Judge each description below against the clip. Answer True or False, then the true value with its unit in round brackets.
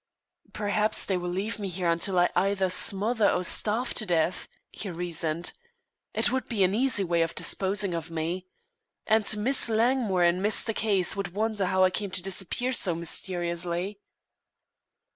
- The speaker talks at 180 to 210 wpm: False (160 wpm)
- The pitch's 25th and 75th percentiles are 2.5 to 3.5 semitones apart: True (3.2 semitones)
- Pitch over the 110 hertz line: True (190 Hz)